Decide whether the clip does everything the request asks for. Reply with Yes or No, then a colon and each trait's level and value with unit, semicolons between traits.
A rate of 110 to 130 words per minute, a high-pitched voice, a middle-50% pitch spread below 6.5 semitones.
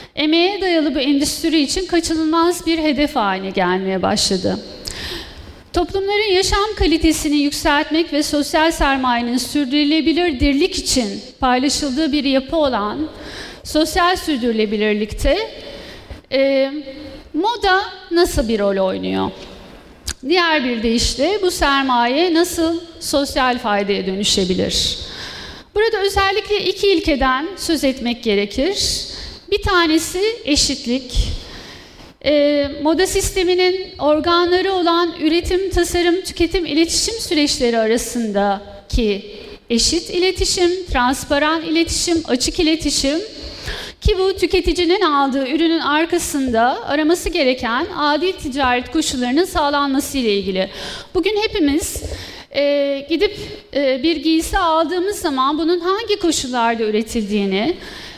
No: average, 100 wpm; very high, 305 Hz; average, 5.1 semitones